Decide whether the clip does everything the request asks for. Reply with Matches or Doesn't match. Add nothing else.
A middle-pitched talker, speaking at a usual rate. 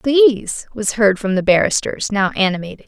Doesn't match